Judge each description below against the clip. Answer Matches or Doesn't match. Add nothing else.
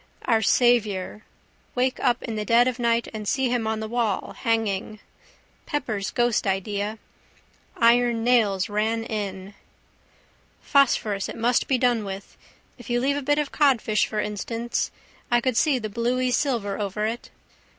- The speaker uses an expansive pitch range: Doesn't match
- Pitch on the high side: Matches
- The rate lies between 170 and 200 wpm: Doesn't match